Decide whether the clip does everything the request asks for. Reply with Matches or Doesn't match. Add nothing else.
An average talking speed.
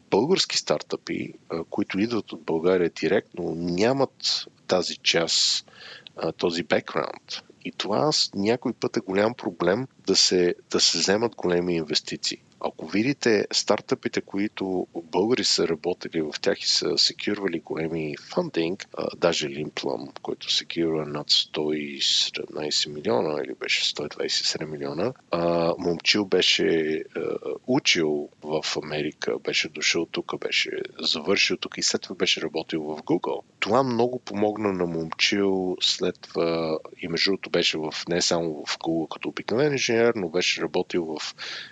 Matches